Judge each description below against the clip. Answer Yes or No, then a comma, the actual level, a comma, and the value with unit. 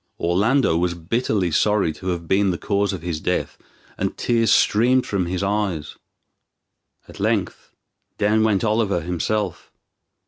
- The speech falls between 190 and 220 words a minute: No, average, 140 wpm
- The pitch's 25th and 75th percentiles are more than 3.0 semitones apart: Yes, average, 3.7 semitones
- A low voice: Yes, low, 100 Hz